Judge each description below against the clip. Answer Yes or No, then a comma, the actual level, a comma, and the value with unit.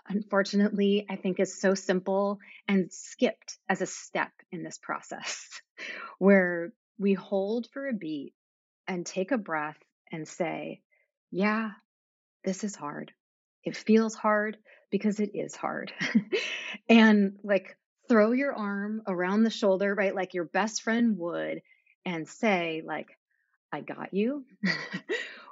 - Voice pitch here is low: No, high, 200 Hz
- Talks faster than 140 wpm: No, slow, 135 wpm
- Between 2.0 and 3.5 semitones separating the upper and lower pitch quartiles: Yes, average, 2.7 semitones